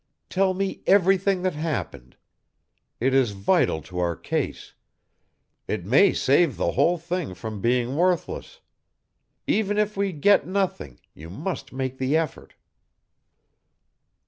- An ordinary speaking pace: No, slow, 125 wpm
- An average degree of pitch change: No, wide, 8.3 semitones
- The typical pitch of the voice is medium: Yes, medium, 155 Hz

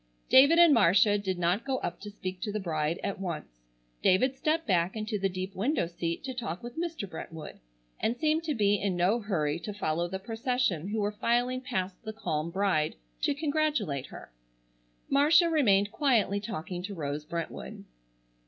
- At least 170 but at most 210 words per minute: Yes, average, 180 wpm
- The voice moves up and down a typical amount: No, wide, 6.2 semitones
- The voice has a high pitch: Yes, high, 205 Hz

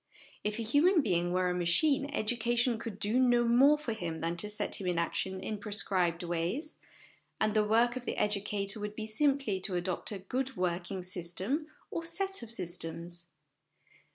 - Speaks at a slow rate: No, average, 180 wpm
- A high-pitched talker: Yes, high, 210 Hz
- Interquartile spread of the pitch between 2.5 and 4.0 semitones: No, average, 5.3 semitones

